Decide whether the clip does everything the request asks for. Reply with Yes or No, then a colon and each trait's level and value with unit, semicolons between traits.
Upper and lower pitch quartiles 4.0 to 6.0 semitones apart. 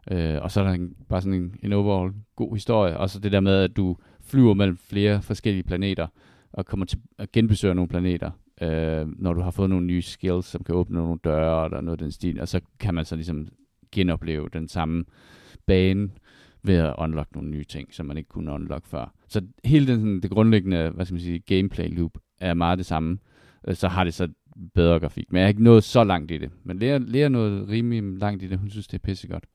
No: average, 3.3 semitones